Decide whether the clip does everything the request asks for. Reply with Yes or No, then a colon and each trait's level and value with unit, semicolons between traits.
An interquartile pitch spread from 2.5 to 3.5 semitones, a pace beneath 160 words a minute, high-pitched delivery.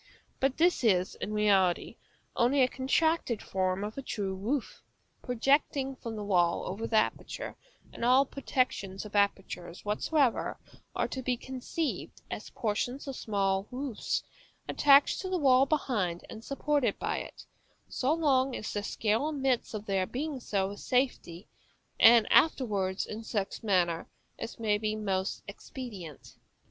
No: average, 5.0 semitones; average, 150 wpm; high, 225 Hz